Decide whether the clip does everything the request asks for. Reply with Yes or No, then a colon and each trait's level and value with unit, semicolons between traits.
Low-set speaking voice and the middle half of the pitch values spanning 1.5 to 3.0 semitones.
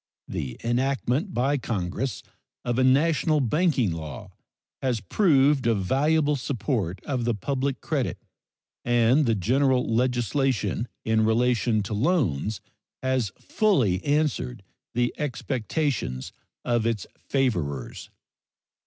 No: low, 125 Hz; average, 4.1 semitones